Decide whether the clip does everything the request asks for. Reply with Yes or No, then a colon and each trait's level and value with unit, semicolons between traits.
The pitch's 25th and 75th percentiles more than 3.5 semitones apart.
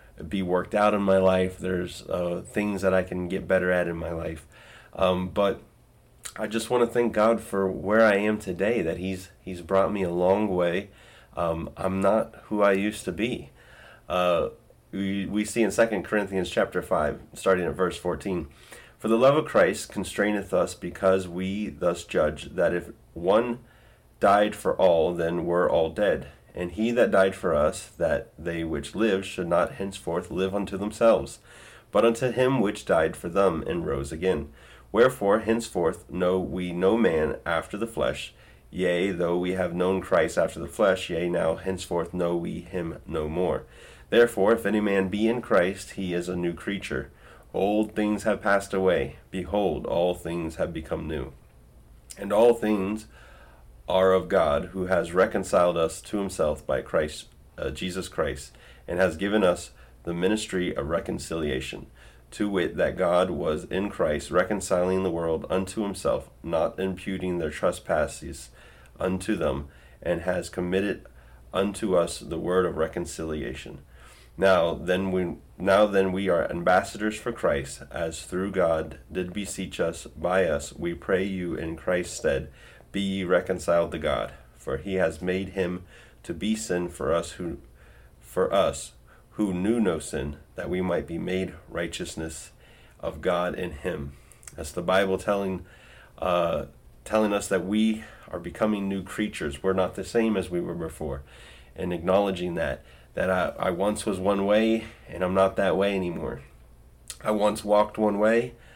No: average, 2.9 semitones